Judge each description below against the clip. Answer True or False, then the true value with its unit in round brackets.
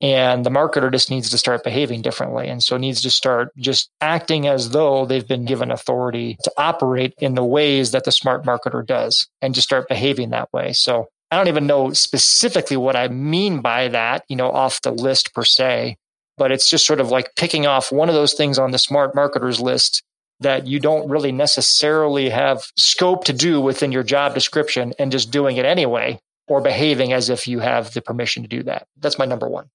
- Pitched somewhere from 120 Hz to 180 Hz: True (135 Hz)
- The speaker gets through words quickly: True (215 wpm)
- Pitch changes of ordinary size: False (2.2 semitones)